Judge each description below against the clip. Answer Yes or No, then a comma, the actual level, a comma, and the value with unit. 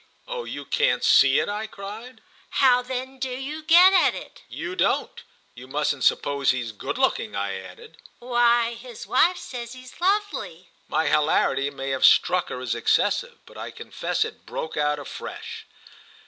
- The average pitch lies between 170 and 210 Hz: No, high, 230 Hz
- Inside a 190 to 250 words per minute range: No, average, 165 wpm